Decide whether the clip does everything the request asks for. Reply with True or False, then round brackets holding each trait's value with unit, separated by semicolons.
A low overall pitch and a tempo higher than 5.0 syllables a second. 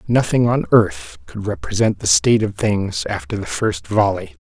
False (110 Hz; 4.7 syllables/s)